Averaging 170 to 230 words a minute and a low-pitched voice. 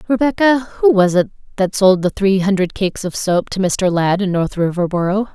No: average, 200 wpm; high, 195 Hz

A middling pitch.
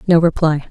Yes: medium, 160 Hz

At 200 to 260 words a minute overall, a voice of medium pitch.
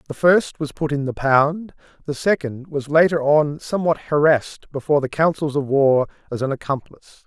No: average, 180 wpm; medium, 145 Hz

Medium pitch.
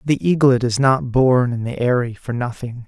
No: low, 125 Hz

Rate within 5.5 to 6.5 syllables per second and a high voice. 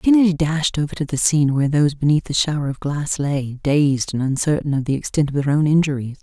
No: 6.0 syllables/s; medium, 145 Hz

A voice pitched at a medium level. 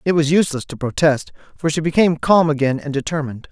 Yes: medium, 150 Hz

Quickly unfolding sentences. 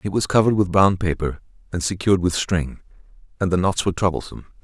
No: average, 195 wpm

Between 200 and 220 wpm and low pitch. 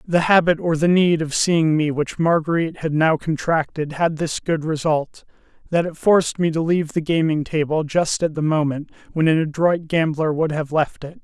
No: fast, 205 wpm; medium, 160 Hz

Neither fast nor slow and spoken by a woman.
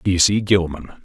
No: average, 175 wpm; male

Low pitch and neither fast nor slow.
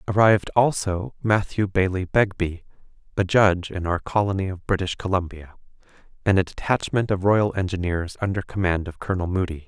Yes: very low, 95 Hz; average, 150 wpm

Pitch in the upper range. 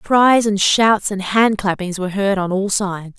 Yes: high, 200 Hz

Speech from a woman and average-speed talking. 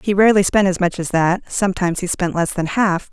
No: female; fast, 250 wpm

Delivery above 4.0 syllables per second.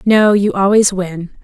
No: 3.8 syllables/s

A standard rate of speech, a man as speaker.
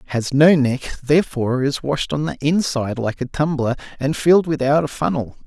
Yes: average, 185 wpm; male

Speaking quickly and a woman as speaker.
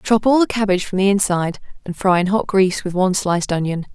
Yes: fast, 245 wpm; female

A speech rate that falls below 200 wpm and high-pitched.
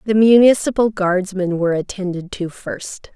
Yes: slow, 135 wpm; high, 195 Hz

